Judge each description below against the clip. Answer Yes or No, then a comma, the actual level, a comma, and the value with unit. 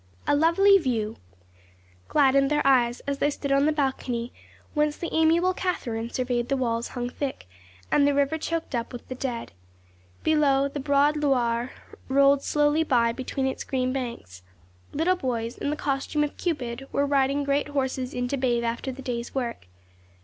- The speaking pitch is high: Yes, very high, 270 Hz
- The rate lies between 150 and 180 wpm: Yes, average, 170 wpm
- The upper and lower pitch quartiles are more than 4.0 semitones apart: No, average, 3.1 semitones